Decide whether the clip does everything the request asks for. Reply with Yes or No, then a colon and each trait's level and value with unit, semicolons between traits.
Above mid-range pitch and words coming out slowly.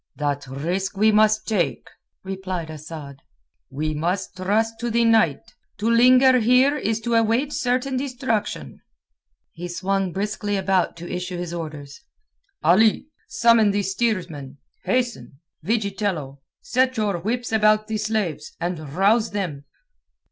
Yes: high, 200 Hz; slow, 130 wpm